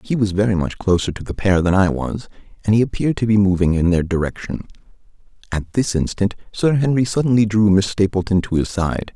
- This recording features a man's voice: Yes, male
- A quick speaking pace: Yes, fast, 210 wpm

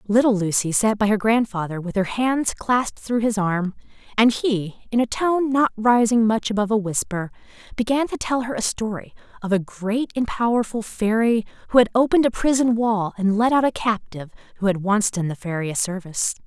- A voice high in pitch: Yes, high, 220 Hz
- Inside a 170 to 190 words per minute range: No, average, 200 wpm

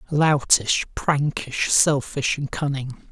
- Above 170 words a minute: No, slow, 95 wpm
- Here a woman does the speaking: No, male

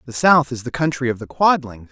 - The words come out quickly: Yes, fast, 250 wpm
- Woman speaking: No, male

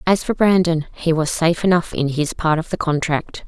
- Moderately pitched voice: Yes, medium, 165 Hz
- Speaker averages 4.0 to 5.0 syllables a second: No, 5.3 syllables/s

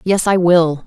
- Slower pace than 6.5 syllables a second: Yes, 3.9 syllables/s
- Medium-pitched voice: Yes, medium, 175 Hz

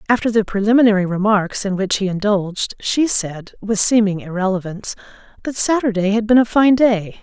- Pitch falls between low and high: No, high, 205 Hz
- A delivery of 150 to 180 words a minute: Yes, average, 165 wpm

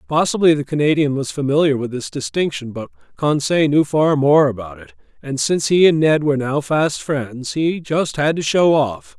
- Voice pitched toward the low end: No, medium, 150 Hz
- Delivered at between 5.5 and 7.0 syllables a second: No, 5.0 syllables/s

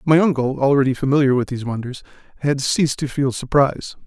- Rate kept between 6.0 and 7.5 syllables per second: Yes, 6.3 syllables/s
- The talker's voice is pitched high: No, low, 135 Hz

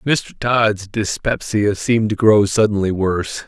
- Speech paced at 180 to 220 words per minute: No, average, 140 wpm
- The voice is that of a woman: No, male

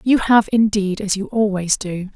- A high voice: Yes, high, 205 Hz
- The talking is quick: No, average, 195 wpm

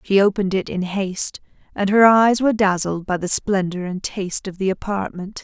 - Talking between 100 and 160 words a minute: No, average, 200 wpm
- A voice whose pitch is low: No, high, 195 Hz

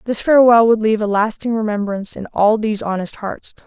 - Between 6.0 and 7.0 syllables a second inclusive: Yes, 6.2 syllables/s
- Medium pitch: No, high, 215 Hz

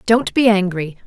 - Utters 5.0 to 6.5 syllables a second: No, 4.6 syllables/s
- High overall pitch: Yes, high, 205 Hz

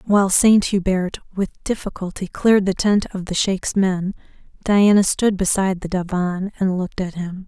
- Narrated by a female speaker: Yes, female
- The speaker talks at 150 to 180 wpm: Yes, average, 170 wpm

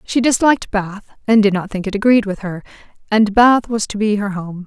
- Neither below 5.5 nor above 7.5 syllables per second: No, 5.3 syllables/s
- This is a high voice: Yes, high, 210 Hz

